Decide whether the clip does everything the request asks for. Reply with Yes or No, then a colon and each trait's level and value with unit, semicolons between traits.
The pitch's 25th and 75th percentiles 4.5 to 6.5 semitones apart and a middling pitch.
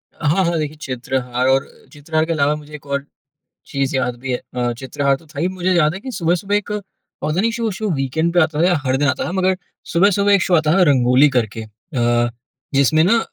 Yes: average, 5.1 semitones; medium, 150 Hz